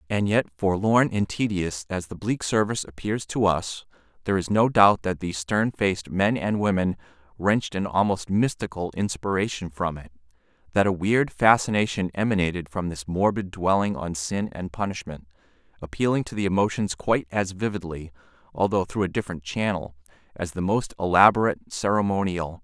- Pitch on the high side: No, very low, 95 Hz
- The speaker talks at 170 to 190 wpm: No, average, 155 wpm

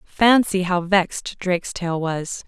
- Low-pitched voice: No, medium, 185 Hz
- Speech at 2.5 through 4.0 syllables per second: Yes, 3.9 syllables/s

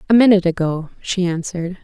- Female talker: Yes, female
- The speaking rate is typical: Yes, average, 165 wpm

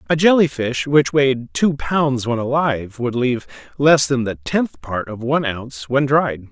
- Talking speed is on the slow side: No, average, 195 wpm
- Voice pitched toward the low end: Yes, low, 130 Hz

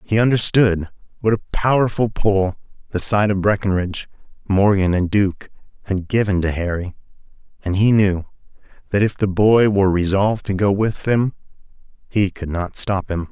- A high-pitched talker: No, low, 100 Hz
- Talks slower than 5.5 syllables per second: Yes, 4.9 syllables/s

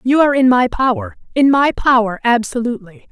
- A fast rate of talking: No, average, 155 wpm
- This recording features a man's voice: No, female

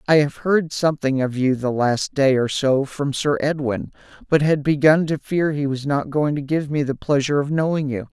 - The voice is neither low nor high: Yes, medium, 145 Hz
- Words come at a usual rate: No, fast, 225 wpm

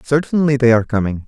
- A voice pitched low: Yes, low, 125 Hz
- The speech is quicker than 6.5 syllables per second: Yes, 7.0 syllables/s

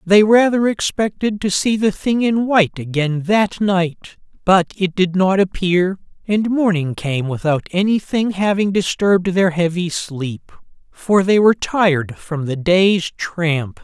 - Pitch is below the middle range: No, medium, 185 Hz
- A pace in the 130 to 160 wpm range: Yes, average, 150 wpm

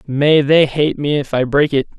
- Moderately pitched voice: Yes, medium, 145 Hz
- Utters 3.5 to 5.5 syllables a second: Yes, 4.6 syllables/s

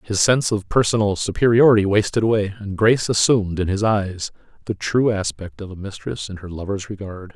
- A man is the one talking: Yes, male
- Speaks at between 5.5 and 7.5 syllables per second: Yes, 5.7 syllables/s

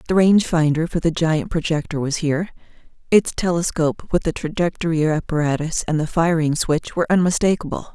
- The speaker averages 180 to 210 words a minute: No, average, 160 wpm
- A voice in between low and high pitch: Yes, medium, 165 Hz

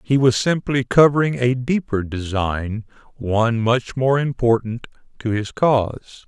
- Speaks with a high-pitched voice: No, low, 120 Hz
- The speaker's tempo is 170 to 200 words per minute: No, slow, 135 wpm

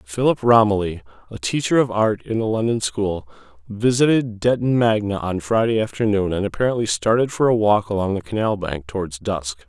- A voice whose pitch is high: No, low, 105 Hz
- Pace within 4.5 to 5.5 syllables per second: Yes, 5.3 syllables/s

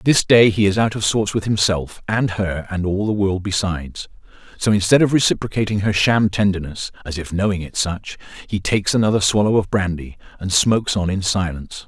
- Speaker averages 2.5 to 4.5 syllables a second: No, 5.5 syllables/s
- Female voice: No, male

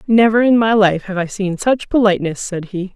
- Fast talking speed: Yes, fast, 225 wpm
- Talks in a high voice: Yes, high, 200 Hz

